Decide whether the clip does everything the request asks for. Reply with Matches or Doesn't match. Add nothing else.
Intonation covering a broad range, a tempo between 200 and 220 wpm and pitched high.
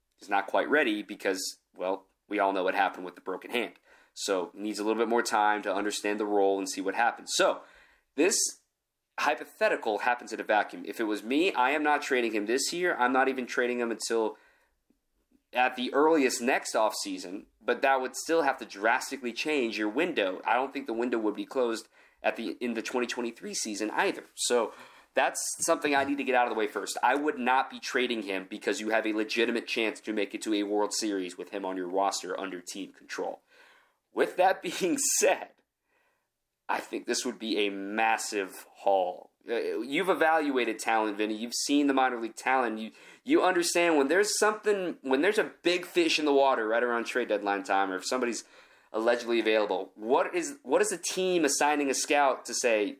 Doesn't match